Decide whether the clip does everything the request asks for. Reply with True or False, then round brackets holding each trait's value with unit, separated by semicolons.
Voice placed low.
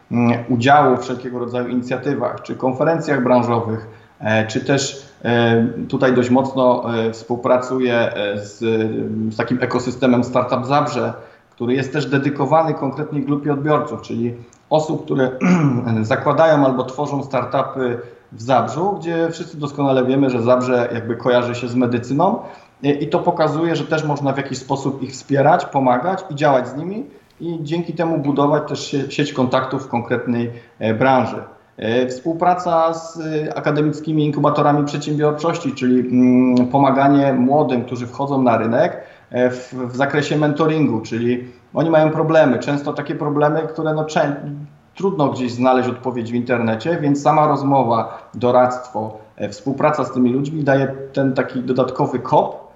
True (130 Hz)